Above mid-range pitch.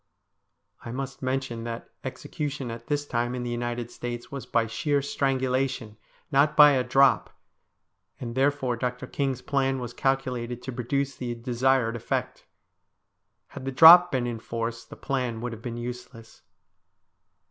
No: low, 125 Hz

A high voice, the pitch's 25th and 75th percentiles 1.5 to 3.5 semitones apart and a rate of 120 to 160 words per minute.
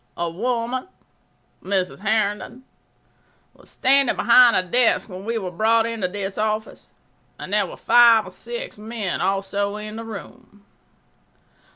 Yes: high, 215 Hz; average, 2.9 semitones; average, 140 wpm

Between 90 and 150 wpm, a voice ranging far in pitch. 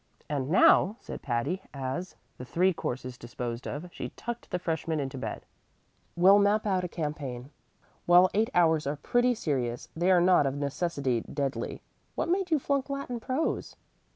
No: average, 165 wpm; wide, 6.6 semitones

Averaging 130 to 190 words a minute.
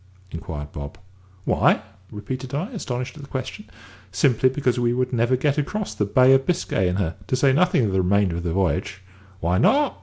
No: average, 200 wpm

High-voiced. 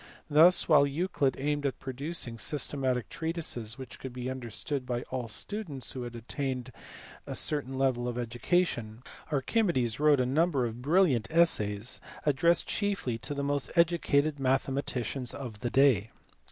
No: low, 135 Hz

